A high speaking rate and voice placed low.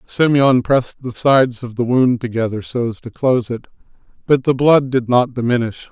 No: average, 195 wpm; low, 125 Hz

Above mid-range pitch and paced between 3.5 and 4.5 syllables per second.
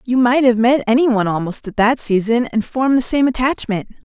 No: high, 240 Hz; 5.6 syllables/s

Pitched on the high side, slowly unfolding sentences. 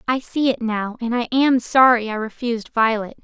No: high, 235 Hz; fast, 205 wpm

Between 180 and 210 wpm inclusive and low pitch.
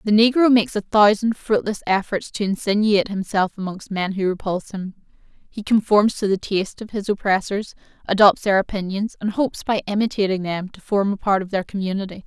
No: average, 185 wpm; high, 200 Hz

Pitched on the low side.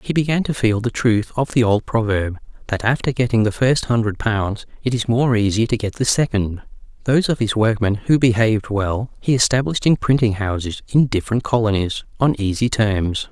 Yes: low, 115 Hz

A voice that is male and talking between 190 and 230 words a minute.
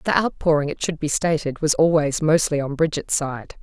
No: female; average, 200 wpm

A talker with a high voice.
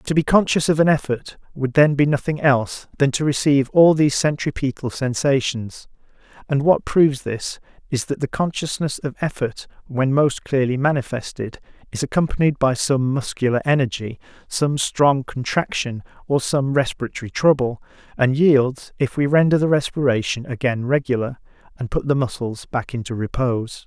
No: low, 135 Hz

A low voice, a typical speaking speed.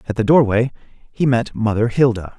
Yes: low, 115 Hz; average, 175 wpm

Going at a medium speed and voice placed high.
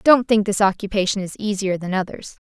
Yes: average, 195 wpm; high, 200 Hz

